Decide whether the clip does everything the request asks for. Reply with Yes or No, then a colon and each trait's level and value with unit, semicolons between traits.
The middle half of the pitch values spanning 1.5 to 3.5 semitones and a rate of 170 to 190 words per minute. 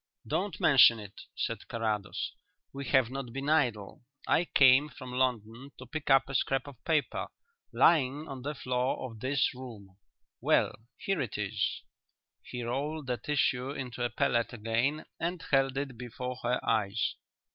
No: average, 3.0 semitones; average, 155 wpm